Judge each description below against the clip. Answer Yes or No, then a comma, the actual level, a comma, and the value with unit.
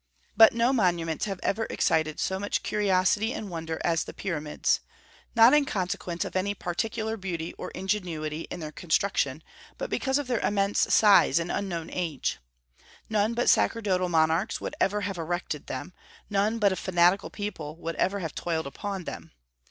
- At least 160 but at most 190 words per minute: Yes, average, 165 wpm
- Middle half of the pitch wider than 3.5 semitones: Yes, average, 3.9 semitones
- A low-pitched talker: No, medium, 185 Hz